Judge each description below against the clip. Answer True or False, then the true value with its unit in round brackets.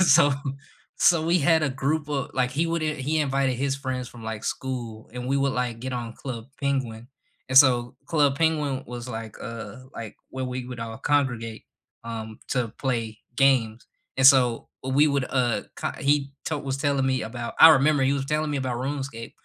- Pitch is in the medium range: False (130 Hz)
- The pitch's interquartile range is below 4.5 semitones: True (2.9 semitones)